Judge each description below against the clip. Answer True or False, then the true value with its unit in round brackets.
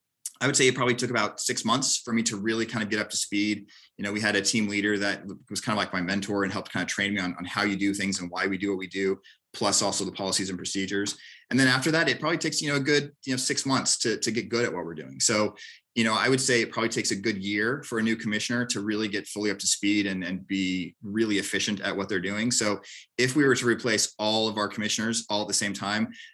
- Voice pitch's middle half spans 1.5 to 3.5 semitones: True (2.9 semitones)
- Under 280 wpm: False (290 wpm)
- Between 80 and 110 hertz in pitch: True (105 Hz)